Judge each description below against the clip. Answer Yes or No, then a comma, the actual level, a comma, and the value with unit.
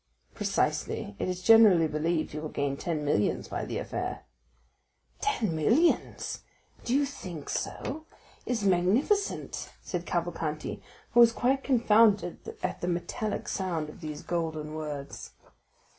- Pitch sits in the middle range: Yes, medium, 175 Hz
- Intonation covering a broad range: Yes, wide, 6.5 semitones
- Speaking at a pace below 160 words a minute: Yes, slow, 135 wpm